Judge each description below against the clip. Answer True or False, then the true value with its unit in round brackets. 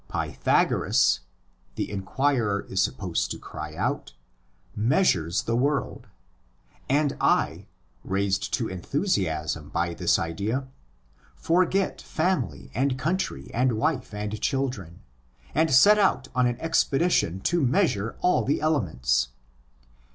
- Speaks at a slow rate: True (115 wpm)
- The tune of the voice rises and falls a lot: True (8.0 semitones)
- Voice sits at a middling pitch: False (120 Hz)